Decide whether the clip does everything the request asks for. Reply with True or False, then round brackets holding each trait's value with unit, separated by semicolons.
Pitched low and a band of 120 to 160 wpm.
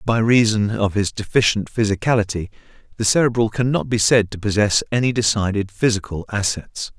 True (105 Hz; 155 wpm)